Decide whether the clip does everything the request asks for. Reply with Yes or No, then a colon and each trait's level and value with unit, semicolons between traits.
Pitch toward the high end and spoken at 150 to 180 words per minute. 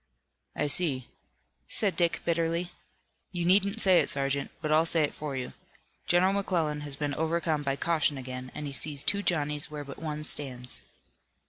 No: medium, 150 Hz; average, 170 wpm